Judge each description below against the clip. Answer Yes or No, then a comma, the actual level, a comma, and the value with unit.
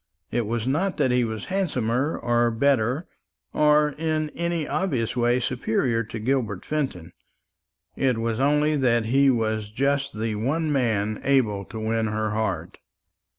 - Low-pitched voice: Yes, low, 125 Hz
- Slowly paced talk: No, average, 150 wpm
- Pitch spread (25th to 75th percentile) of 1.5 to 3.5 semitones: No, average, 4.3 semitones